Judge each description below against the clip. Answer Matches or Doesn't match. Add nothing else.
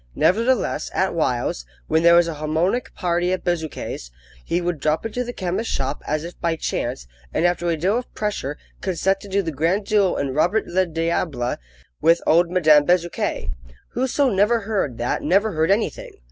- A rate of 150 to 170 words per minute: Doesn't match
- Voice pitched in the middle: Matches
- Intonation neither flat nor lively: Matches